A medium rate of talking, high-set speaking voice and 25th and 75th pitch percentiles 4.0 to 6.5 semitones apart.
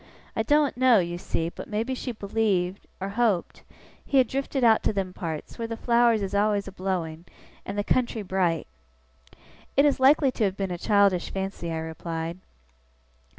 Yes: average, 180 wpm; high, 200 Hz; average, 4.8 semitones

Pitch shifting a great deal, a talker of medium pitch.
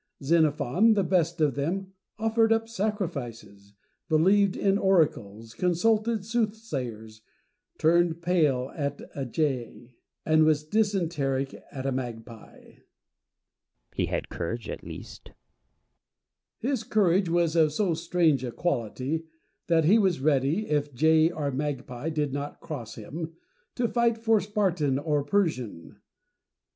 Yes: wide, 6.2 semitones; medium, 160 Hz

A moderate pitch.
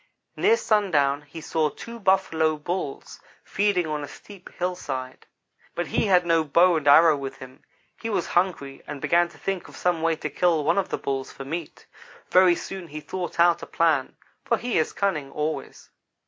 Yes: medium, 165 Hz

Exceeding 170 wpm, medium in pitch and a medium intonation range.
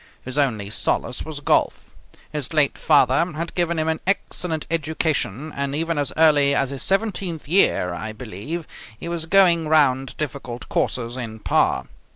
No: average, 160 wpm; medium, 150 Hz; average, 4.3 semitones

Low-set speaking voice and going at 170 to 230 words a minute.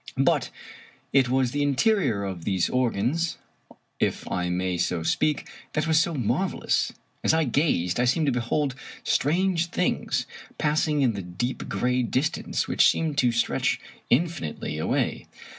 No: low, 130 Hz; average, 155 wpm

